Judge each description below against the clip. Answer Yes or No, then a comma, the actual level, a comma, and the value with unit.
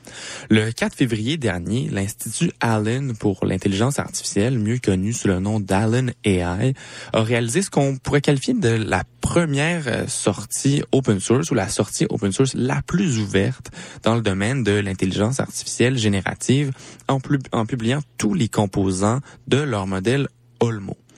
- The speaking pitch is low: Yes, low, 115 Hz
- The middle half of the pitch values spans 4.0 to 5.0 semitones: Yes, average, 4.5 semitones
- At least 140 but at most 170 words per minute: Yes, average, 155 wpm